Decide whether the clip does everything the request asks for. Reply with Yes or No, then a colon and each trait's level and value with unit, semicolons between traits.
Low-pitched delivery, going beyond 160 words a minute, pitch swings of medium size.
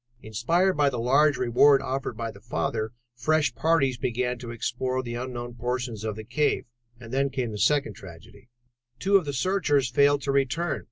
Yes: low, 130 Hz; average, 180 wpm; average, 3.3 semitones